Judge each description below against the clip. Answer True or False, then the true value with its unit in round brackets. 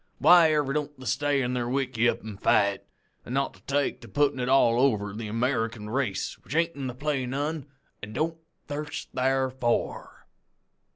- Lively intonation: False (3.5 semitones)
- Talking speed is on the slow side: False (165 wpm)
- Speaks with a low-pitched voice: True (130 Hz)